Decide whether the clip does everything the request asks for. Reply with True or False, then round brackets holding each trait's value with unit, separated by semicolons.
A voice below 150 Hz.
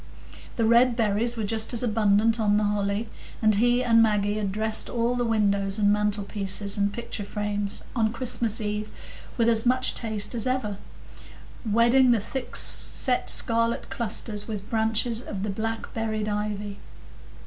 False (220 Hz)